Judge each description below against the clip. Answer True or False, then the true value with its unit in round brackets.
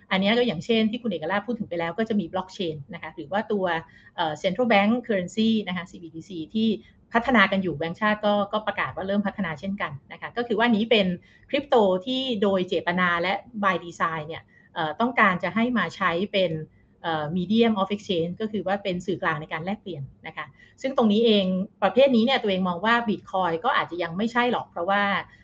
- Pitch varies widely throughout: False (4.4 semitones)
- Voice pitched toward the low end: False (195 Hz)